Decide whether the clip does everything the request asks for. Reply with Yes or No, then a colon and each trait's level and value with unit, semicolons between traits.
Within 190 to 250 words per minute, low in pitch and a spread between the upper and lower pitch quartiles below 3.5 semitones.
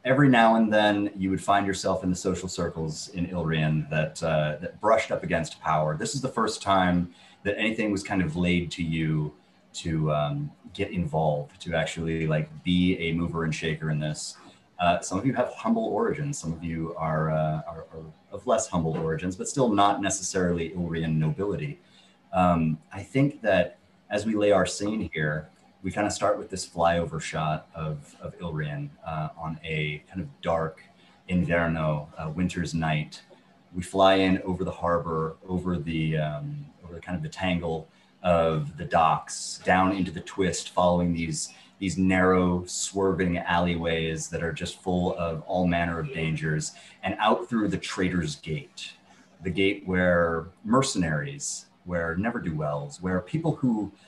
No: average, 170 wpm; very low, 85 Hz; average, 2.9 semitones